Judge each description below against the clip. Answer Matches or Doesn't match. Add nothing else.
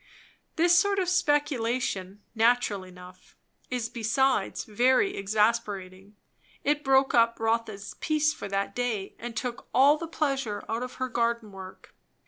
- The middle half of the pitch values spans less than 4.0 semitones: Doesn't match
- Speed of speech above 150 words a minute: Doesn't match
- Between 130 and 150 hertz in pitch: Doesn't match